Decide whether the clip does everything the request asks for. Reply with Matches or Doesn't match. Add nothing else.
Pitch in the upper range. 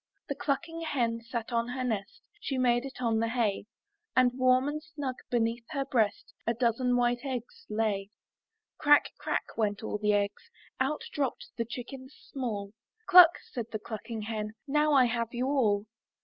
Matches